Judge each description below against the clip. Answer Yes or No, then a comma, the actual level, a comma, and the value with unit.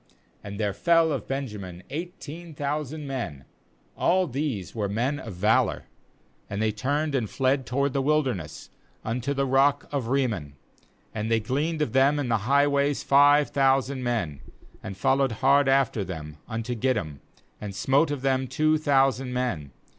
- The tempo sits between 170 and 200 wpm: No, average, 160 wpm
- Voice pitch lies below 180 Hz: Yes, low, 135 Hz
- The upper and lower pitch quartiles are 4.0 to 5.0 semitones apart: Yes, average, 4.7 semitones